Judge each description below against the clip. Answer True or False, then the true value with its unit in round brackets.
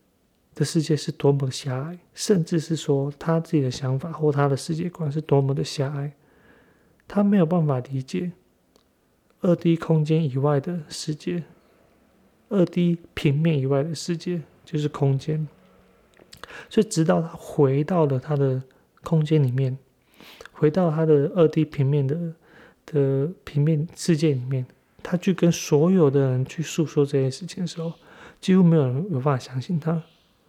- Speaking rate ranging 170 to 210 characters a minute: False (230 characters per minute)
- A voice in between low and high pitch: True (155 Hz)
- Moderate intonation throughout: True (3.1 semitones)